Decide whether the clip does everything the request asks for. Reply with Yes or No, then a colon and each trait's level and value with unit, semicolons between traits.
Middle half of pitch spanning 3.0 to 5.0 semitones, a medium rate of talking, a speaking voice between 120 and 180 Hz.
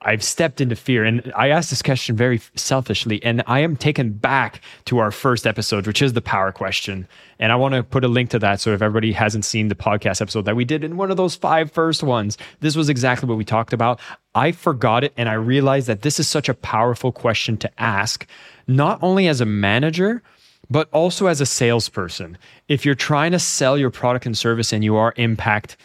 No: average, 4.5 semitones; fast, 225 wpm; low, 125 Hz